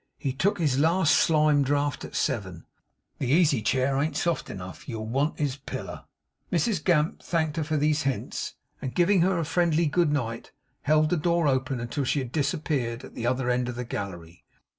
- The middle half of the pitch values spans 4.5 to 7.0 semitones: No, average, 4.1 semitones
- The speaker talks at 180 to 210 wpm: Yes, average, 190 wpm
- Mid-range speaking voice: Yes, medium, 145 Hz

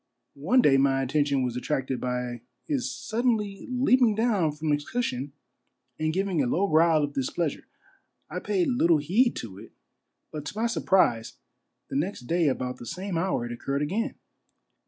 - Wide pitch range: Yes, wide, 7.5 semitones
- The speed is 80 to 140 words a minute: No, average, 165 wpm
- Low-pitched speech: No, medium, 155 Hz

